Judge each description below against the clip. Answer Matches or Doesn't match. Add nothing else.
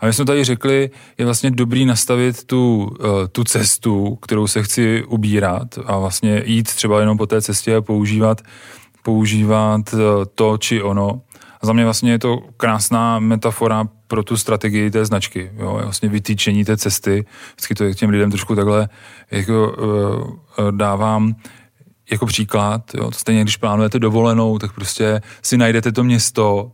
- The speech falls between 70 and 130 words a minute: Doesn't match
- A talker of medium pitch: Doesn't match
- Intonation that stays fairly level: Matches